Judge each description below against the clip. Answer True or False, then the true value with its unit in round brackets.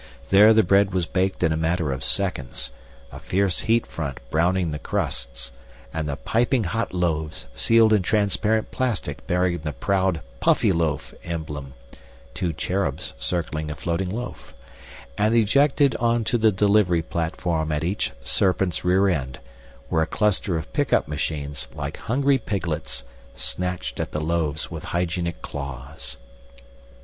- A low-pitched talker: True (90 Hz)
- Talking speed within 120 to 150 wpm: True (140 wpm)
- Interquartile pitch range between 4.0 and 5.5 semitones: True (4.6 semitones)